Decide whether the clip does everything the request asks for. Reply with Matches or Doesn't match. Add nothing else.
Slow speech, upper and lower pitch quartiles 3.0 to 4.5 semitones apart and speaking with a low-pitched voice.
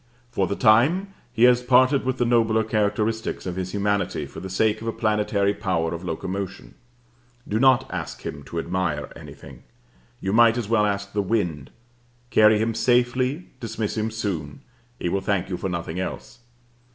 Doesn't match